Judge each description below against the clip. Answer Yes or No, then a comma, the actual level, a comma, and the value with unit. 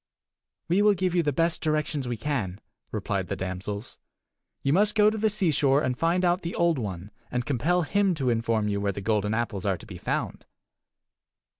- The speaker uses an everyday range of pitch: No, wide, 8.8 semitones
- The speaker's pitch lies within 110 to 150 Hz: Yes, low, 135 Hz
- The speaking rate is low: No, average, 195 wpm